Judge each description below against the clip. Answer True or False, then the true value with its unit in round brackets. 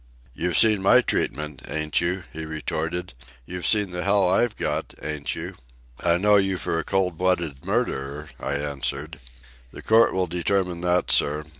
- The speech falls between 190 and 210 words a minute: False (165 wpm)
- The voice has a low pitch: True (90 Hz)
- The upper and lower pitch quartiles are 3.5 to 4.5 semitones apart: True (3.9 semitones)